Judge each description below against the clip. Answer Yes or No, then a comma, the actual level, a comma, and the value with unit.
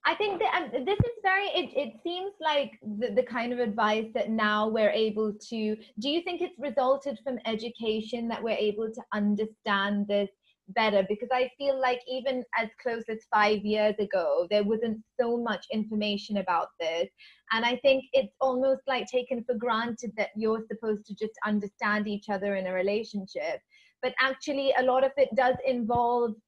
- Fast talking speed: No, average, 185 wpm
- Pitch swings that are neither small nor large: Yes, average, 3.7 semitones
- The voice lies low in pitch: No, high, 230 Hz